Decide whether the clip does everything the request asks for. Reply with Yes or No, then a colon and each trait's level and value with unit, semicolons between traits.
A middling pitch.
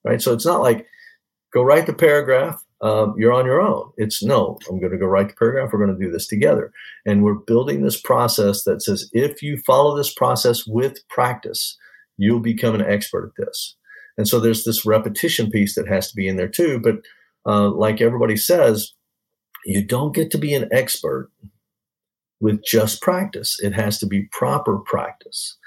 No: low, 110 Hz